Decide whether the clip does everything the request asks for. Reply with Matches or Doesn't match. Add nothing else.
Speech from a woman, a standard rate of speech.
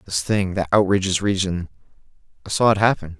Doesn't match